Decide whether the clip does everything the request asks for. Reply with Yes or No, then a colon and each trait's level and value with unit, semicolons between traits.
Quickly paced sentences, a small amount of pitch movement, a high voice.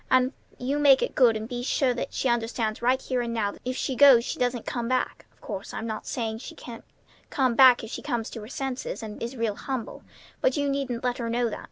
Yes: fast, 245 wpm; narrow, 2.2 semitones; high, 245 Hz